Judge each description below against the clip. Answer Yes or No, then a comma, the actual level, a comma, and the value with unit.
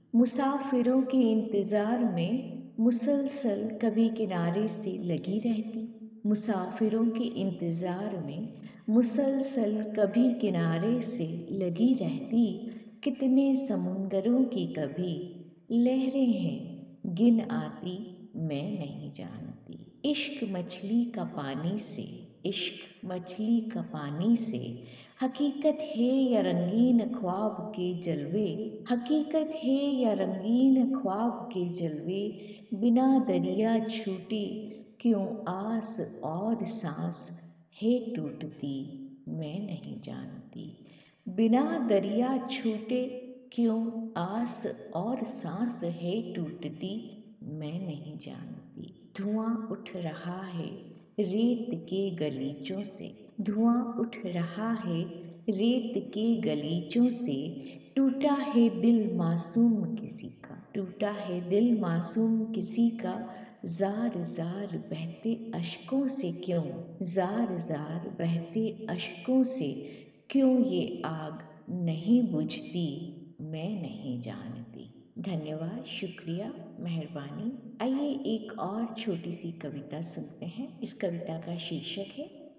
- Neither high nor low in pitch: No, high, 215 Hz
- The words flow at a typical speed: No, slow, 105 wpm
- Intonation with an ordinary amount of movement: Yes, average, 4.9 semitones